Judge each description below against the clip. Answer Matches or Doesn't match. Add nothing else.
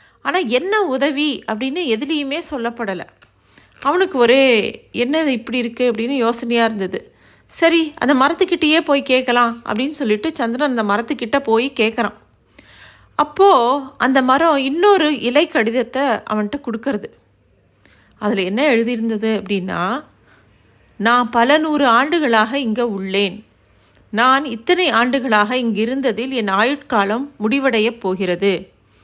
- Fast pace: Doesn't match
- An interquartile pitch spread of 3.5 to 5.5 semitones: Matches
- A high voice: Matches